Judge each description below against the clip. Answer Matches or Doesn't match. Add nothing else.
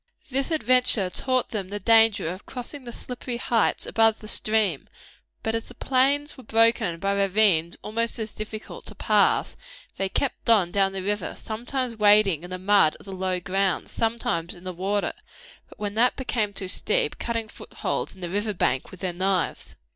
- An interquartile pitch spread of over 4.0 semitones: Doesn't match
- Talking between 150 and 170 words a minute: Doesn't match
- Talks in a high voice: Matches